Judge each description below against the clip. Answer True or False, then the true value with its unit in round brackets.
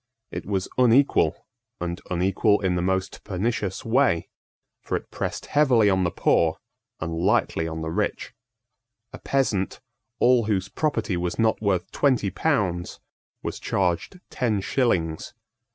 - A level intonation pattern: False (4.9 semitones)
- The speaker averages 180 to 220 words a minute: False (135 wpm)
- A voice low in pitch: True (100 Hz)